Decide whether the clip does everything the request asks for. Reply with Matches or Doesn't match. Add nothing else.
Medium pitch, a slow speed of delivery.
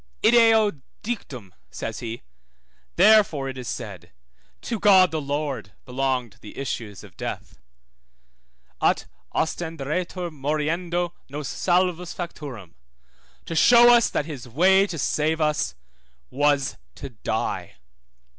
Matches